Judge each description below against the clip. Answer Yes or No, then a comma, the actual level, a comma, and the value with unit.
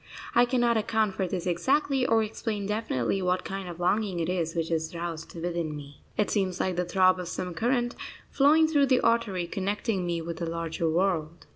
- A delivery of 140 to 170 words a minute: No, average, 195 wpm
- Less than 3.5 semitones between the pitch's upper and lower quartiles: No, average, 4.7 semitones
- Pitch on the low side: No, medium, 185 Hz